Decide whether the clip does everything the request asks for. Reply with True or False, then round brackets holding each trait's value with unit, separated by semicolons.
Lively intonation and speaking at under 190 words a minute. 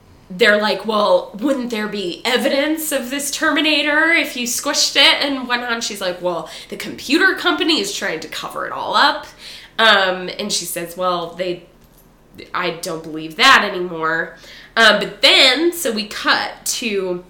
True (7.6 semitones; 165 wpm)